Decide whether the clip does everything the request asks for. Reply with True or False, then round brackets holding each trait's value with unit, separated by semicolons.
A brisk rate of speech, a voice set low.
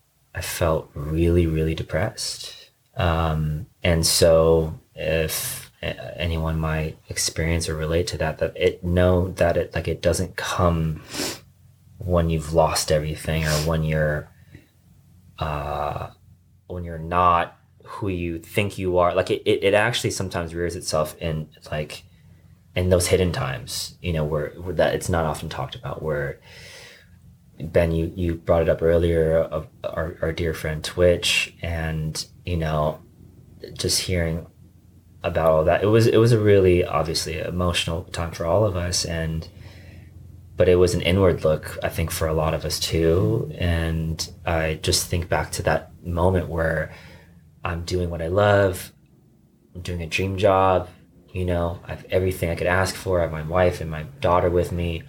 False (165 wpm; 85 Hz)